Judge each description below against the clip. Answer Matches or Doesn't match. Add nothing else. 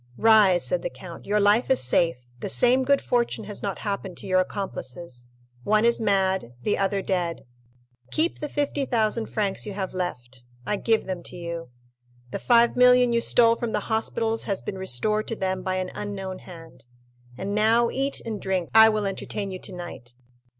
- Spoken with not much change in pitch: Doesn't match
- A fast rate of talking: Doesn't match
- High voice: Matches